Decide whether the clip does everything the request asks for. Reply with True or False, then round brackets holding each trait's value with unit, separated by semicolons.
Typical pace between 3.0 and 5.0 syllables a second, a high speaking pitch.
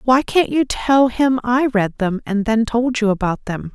True (4.2 syllables/s; 235 Hz)